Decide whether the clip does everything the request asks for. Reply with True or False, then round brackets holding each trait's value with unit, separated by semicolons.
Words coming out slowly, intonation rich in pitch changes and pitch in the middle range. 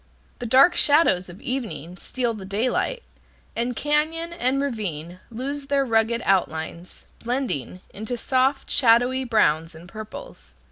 False (130 wpm; 6.3 semitones; 235 Hz)